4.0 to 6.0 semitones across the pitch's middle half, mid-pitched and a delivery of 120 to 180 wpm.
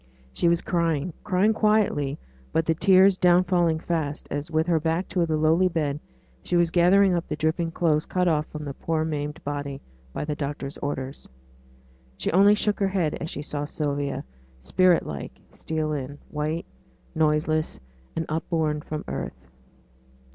No: average, 2.8 semitones; medium, 160 Hz; average, 165 wpm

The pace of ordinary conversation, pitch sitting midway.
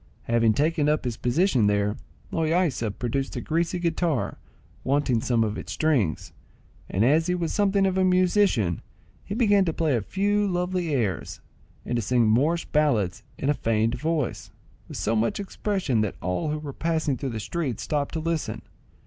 Yes: average, 175 wpm; medium, 150 Hz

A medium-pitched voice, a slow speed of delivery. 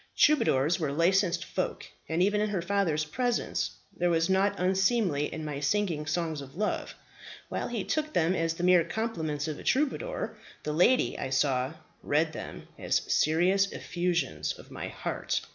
No: medium, 175 Hz; average, 165 wpm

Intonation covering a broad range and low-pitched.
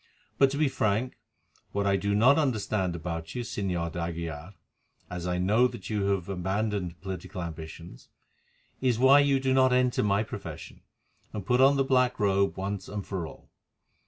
Yes: wide, 5.8 semitones; low, 100 Hz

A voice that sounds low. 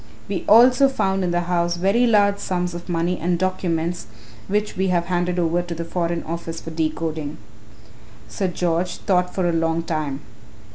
No: medium, 175 Hz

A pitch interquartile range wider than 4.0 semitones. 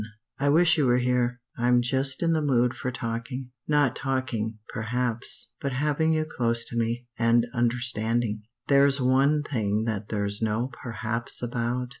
No: average, 2.8 semitones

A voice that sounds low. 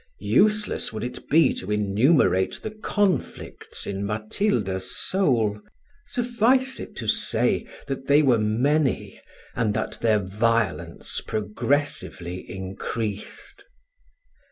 Yes: low, 115 Hz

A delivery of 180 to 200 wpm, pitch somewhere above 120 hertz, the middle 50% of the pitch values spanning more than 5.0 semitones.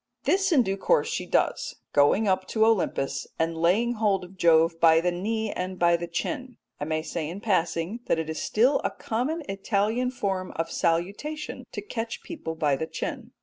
Yes: average, 190 wpm; high, 190 Hz; wide, 5.5 semitones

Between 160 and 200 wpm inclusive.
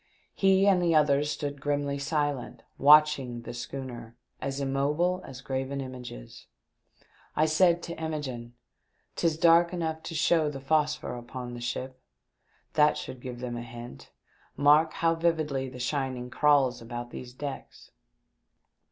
No: average, 140 wpm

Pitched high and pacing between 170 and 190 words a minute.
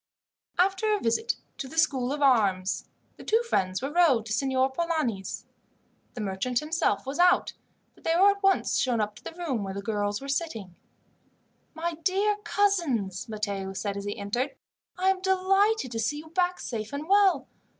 Yes: very high, 275 Hz; average, 180 wpm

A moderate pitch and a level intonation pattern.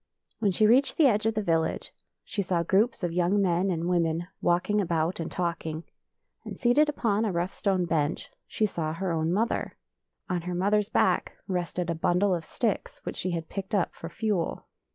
No: medium, 180 Hz; average, 3.6 semitones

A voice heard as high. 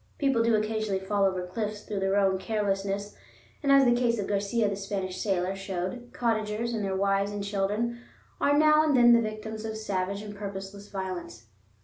Yes: high, 205 Hz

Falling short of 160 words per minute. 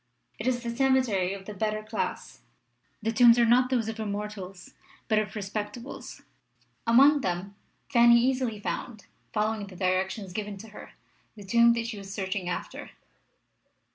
Yes: average, 150 wpm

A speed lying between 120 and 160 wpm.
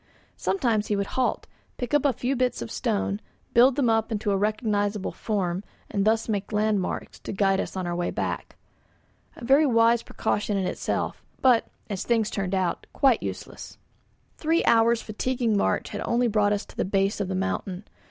No: average, 185 wpm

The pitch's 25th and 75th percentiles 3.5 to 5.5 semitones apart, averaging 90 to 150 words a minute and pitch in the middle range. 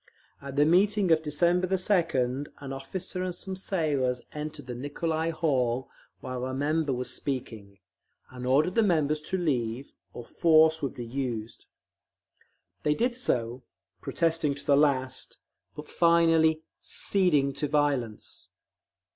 Yes: average, 4.3 semitones; slow, 135 wpm; medium, 150 Hz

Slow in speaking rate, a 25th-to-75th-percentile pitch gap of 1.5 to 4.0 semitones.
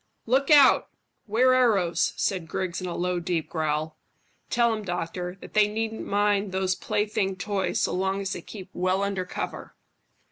No: average, 170 wpm; average, 2.8 semitones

